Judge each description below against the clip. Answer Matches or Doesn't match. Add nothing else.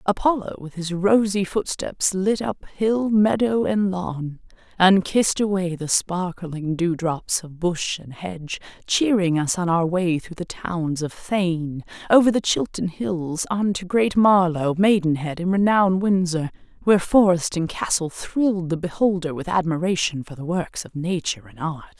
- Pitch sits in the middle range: Matches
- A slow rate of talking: Doesn't match